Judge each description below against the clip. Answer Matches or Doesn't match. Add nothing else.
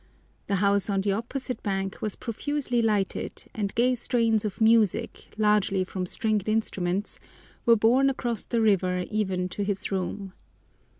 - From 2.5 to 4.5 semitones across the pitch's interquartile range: Matches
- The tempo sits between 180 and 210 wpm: Doesn't match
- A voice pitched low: Doesn't match